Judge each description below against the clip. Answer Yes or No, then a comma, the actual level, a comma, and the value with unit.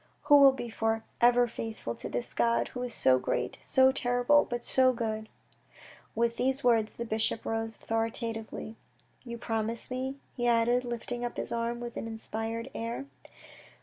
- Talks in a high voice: Yes, high, 235 Hz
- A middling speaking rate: Yes, average, 180 wpm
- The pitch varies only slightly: Yes, narrow, 1.7 semitones